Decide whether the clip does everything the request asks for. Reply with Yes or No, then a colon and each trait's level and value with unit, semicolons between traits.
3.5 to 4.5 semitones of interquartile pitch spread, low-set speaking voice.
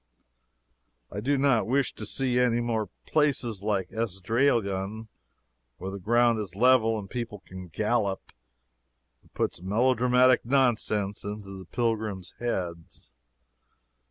Yes: average, 3.8 semitones; low, 110 Hz